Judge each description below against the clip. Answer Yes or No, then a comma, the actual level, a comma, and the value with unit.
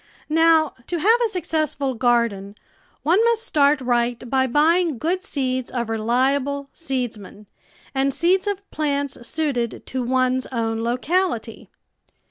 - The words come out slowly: Yes, slow, 125 wpm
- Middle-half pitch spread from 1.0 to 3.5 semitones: No, average, 5.0 semitones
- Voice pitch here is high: Yes, very high, 270 Hz